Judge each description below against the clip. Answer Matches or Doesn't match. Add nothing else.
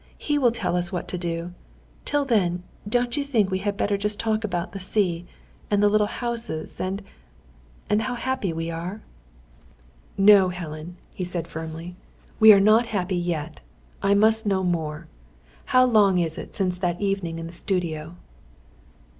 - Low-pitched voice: Doesn't match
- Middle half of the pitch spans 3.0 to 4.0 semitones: Matches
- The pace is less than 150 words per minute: Doesn't match